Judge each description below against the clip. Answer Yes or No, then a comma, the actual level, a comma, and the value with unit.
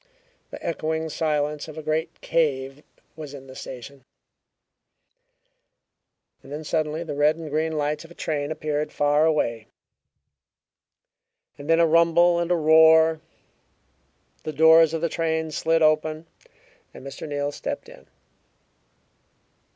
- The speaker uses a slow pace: Yes, slow, 130 wpm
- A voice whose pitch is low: No, medium, 155 Hz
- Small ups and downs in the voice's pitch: Yes, narrow, 1.6 semitones